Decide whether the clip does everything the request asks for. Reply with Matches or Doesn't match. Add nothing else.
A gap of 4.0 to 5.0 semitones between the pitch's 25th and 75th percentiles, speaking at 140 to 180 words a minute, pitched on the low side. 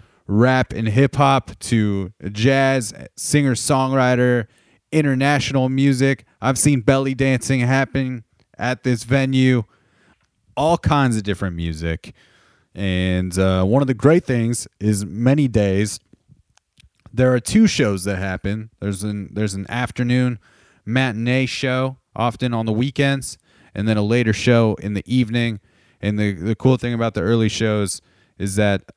Matches